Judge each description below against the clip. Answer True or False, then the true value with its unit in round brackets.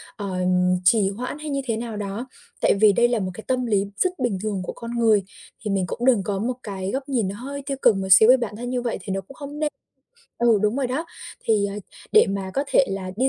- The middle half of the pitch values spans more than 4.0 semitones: True (4.4 semitones)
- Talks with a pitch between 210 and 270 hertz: True (225 Hz)